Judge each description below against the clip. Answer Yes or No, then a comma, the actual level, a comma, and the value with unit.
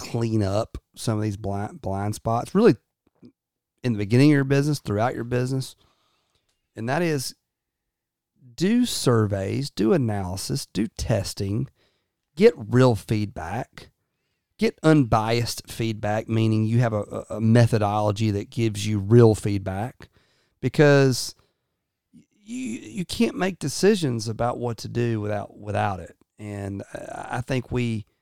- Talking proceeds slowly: Yes, slow, 130 wpm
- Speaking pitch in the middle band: No, low, 115 Hz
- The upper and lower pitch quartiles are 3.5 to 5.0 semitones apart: Yes, average, 3.8 semitones